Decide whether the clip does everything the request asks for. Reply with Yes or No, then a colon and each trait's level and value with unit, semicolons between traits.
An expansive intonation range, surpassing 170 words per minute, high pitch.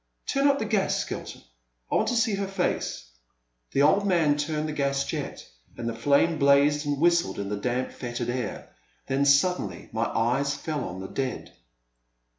No: wide, 5.7 semitones; average, 180 wpm; medium, 140 Hz